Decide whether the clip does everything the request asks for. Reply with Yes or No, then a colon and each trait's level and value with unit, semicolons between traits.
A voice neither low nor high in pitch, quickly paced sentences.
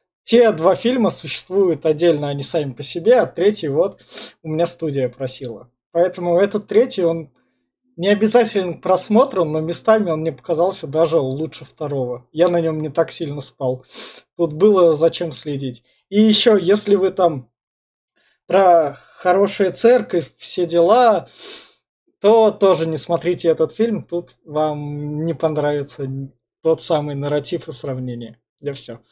No: medium, 165 Hz; average, 145 wpm